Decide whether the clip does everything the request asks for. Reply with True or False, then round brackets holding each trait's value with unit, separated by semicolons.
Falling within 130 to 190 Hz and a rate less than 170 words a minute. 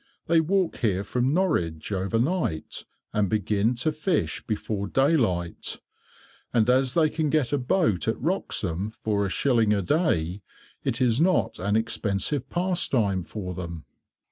False (115 Hz; 145 wpm)